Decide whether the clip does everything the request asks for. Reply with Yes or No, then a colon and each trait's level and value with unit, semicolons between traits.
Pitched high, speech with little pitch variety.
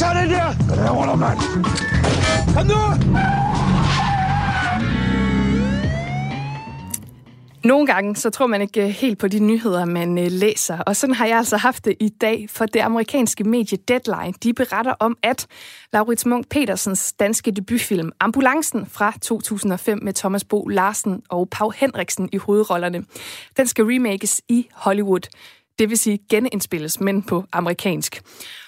No: high, 210 Hz; average, 4.0 semitones